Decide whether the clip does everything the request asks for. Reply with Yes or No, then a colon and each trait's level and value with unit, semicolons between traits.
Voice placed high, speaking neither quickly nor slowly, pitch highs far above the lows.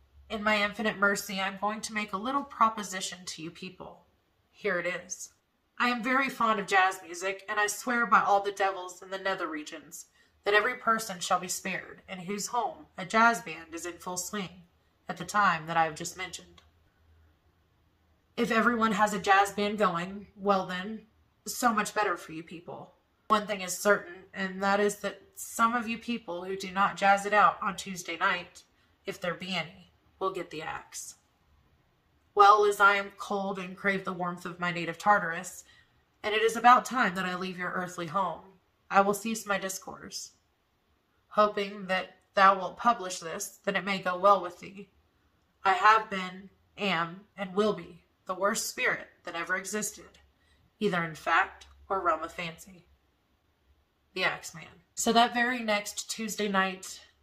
No: high, 195 Hz; average, 185 wpm; average, 2.9 semitones